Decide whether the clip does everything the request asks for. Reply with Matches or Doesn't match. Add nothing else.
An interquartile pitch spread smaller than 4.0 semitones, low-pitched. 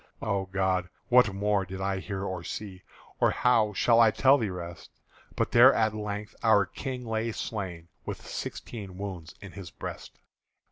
Matches